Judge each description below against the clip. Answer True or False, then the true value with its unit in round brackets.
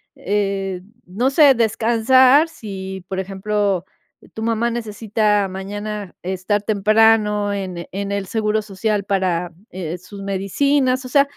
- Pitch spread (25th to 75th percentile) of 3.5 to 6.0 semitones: False (2.6 semitones)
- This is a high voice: True (205 Hz)